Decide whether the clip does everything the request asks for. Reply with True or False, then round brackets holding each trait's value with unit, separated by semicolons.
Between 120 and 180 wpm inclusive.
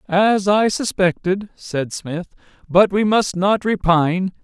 True (135 wpm)